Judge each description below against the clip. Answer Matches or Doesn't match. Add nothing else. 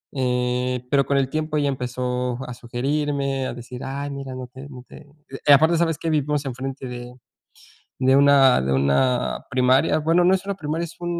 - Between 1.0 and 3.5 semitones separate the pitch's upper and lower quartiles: Matches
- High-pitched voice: Doesn't match